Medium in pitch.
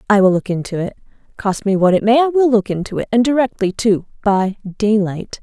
No: high, 210 Hz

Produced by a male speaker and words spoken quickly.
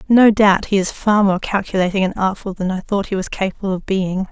No: female; fast, 235 wpm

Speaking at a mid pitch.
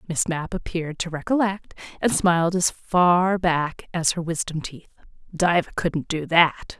Yes: medium, 170 Hz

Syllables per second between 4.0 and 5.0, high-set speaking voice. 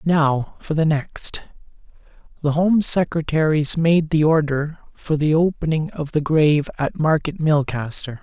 No: 4.2 syllables/s; medium, 155 Hz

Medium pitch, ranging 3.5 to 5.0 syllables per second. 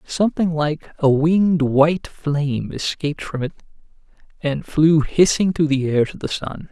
Yes: medium, 155 Hz; 4.6 syllables/s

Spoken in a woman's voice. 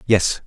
No: male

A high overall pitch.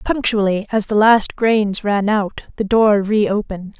Yes: high, 210 Hz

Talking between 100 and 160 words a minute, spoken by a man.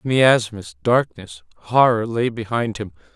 Yes: slow, 135 wpm; male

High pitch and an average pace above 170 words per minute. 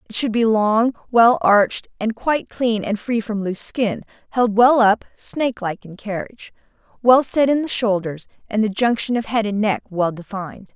Yes: high, 205 Hz; average, 190 wpm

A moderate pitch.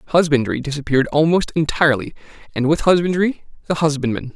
Yes: medium, 150 Hz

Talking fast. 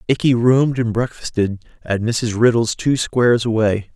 No: average, 150 wpm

